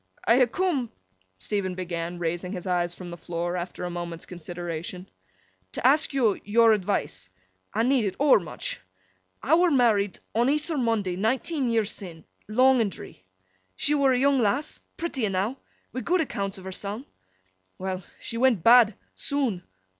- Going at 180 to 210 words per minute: No, average, 150 wpm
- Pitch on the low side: No, high, 210 Hz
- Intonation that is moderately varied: No, wide, 6.3 semitones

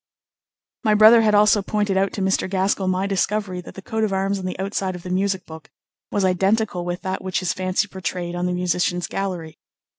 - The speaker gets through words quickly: Yes, fast, 210 wpm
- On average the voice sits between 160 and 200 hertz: Yes, high, 190 Hz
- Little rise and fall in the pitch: Yes, narrow, 1.8 semitones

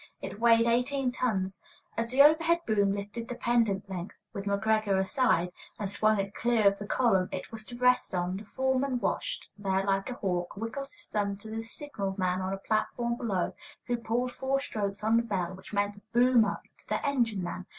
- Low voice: No, high, 215 Hz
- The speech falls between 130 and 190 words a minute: No, average, 200 wpm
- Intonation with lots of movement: No, average, 3.8 semitones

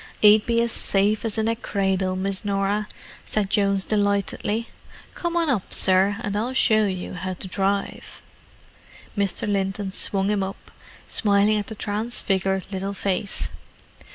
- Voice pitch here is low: No, high, 200 Hz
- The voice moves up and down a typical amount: No, narrow, 1.8 semitones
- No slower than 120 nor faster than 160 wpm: Yes, average, 150 wpm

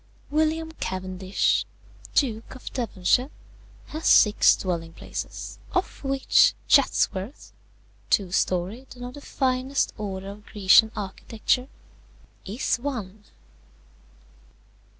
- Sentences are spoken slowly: Yes, slow, 95 wpm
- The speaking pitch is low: No, high, 225 Hz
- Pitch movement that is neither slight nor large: No, wide, 5.9 semitones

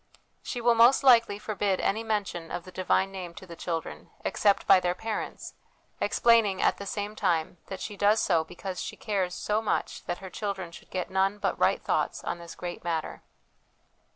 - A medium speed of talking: Yes, average, 190 wpm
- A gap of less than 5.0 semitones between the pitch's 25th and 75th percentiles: Yes, average, 3.0 semitones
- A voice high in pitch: Yes, high, 195 Hz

